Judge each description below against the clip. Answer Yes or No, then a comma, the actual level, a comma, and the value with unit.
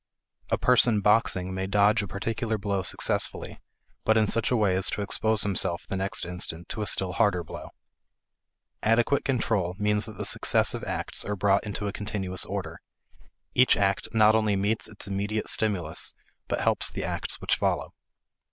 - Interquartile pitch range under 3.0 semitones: Yes, narrow, 2.4 semitones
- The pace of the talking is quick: No, average, 170 wpm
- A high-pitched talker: No, low, 100 Hz